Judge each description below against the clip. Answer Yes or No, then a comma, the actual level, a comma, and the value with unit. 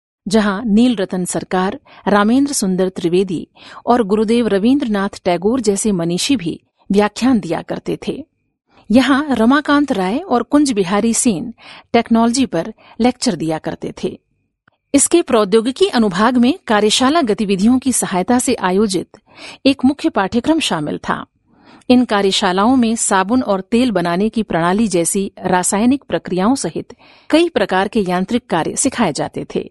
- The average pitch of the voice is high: Yes, high, 220 Hz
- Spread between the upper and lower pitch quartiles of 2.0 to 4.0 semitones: No, average, 4.6 semitones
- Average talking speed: Yes, average, 135 wpm